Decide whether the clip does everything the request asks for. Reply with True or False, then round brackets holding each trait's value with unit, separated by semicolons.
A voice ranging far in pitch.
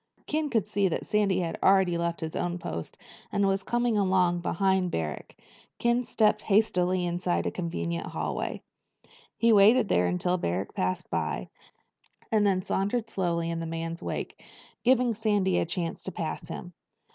False (3.8 semitones)